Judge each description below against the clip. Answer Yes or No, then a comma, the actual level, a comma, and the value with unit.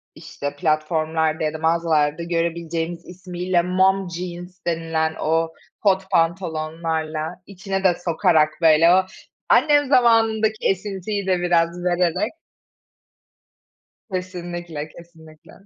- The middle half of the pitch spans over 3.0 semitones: No, narrow, 2.4 semitones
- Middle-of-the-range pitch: Yes, medium, 170 Hz